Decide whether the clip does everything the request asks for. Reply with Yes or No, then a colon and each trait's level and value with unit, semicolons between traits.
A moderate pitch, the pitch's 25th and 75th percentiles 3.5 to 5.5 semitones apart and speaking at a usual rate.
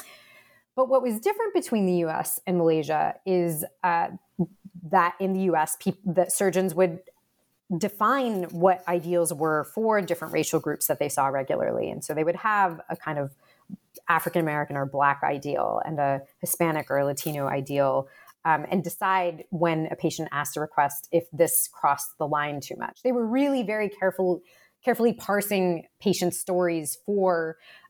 Yes: medium, 175 Hz; average, 4.0 semitones; average, 165 wpm